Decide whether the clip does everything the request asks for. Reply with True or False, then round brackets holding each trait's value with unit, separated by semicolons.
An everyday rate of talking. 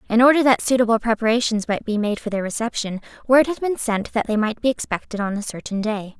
False (235 wpm)